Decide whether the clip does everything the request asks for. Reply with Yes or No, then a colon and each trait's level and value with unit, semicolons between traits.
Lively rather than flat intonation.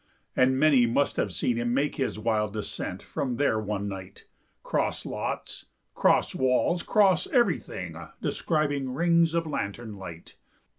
Yes: wide, 6.2 semitones